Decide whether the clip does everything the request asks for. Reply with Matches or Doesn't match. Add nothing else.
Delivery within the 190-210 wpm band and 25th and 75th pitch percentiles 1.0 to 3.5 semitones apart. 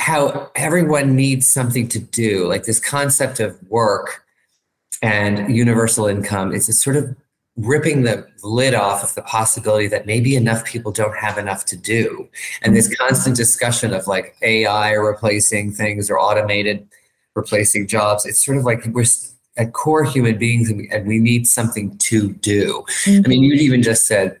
Doesn't match